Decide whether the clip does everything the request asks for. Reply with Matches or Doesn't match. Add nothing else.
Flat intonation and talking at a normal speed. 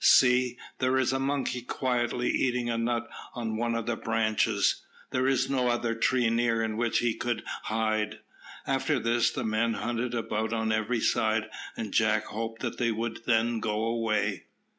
Matches